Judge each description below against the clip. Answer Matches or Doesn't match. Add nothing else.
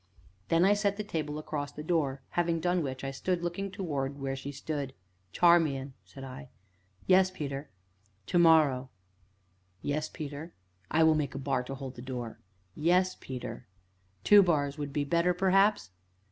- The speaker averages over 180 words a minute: Doesn't match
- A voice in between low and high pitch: Matches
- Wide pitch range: Doesn't match